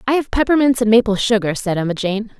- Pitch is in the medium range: No, high, 220 Hz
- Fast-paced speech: Yes, fast, 225 wpm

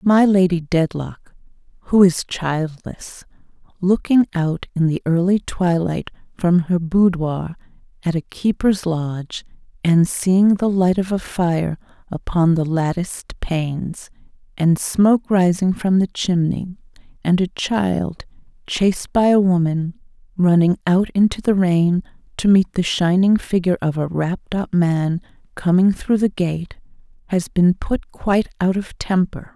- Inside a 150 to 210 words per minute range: No, average, 140 wpm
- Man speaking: No, female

